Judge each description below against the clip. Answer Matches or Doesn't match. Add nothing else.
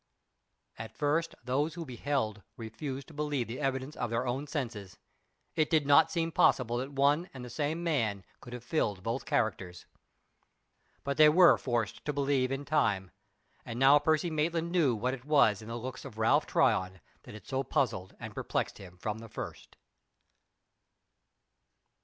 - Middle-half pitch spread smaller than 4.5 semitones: Doesn't match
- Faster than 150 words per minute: Matches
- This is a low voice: Matches